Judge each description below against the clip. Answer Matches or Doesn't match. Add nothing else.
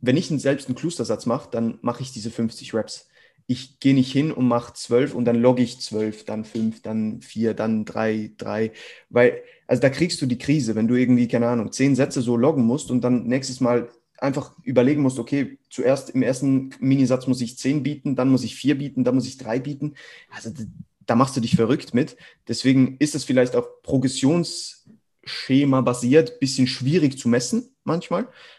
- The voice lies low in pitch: Matches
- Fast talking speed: Matches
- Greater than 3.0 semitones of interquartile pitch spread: Doesn't match